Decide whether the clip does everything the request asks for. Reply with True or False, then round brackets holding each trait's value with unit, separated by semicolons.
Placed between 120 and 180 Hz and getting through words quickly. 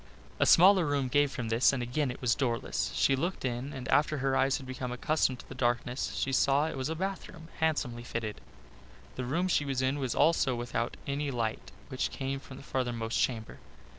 True (135 Hz; 210 wpm)